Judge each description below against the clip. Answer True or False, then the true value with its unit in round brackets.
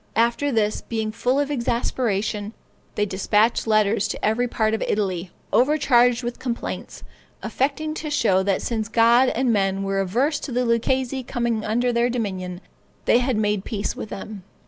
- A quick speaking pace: False (165 wpm)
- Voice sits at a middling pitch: False (230 Hz)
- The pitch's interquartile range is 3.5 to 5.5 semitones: False (3.0 semitones)